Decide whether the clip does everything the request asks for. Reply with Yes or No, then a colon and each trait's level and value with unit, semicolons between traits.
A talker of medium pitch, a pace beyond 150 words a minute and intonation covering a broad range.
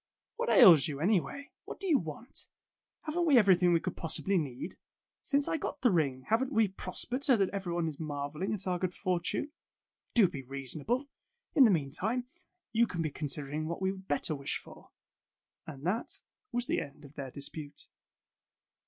Yes: medium, 180 Hz; average, 180 wpm; wide, 7.7 semitones